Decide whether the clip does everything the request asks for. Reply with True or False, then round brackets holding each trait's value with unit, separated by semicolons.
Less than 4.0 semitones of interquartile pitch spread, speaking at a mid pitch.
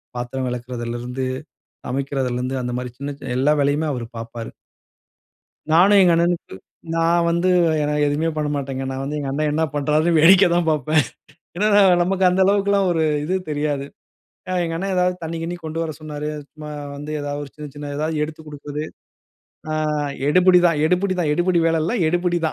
True (3.6 semitones; 155 Hz)